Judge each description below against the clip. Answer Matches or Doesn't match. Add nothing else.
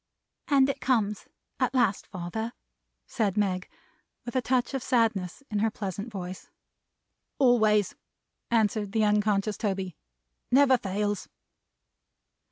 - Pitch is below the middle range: Doesn't match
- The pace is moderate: Doesn't match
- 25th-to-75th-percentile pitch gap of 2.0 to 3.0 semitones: Doesn't match